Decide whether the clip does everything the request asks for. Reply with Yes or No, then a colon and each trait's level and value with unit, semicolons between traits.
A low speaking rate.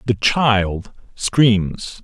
Yes: slow, 90 wpm